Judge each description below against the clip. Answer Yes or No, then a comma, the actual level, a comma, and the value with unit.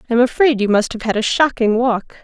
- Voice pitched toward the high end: Yes, high, 235 Hz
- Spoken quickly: Yes, fast, 270 wpm